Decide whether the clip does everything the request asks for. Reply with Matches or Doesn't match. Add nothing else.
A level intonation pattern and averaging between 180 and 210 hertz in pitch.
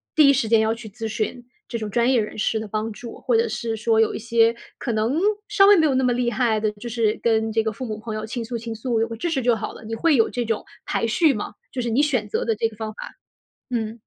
Doesn't match